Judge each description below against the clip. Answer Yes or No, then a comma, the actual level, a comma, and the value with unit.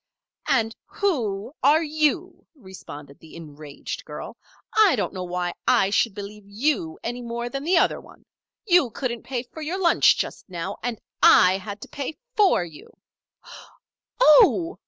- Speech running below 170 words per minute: Yes, average, 155 wpm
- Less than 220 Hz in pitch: No, high, 235 Hz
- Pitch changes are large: Yes, wide, 8.4 semitones